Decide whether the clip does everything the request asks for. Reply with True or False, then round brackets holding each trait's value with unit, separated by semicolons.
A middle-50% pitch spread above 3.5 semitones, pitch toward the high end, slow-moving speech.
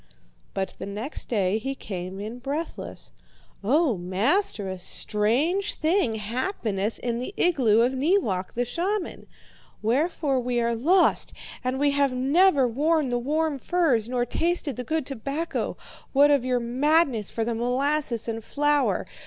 False (5.2 semitones; 255 Hz; 145 wpm)